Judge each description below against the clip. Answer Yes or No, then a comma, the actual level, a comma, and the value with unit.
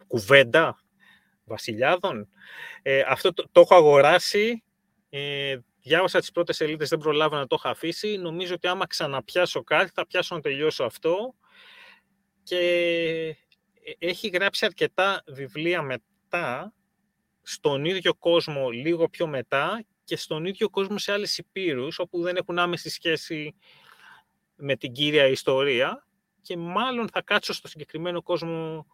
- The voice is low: No, medium, 175 Hz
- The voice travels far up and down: No, average, 4.1 semitones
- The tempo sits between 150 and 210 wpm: No, average, 135 wpm